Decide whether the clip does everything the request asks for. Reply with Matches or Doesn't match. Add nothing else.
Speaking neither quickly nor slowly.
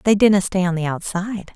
Doesn't match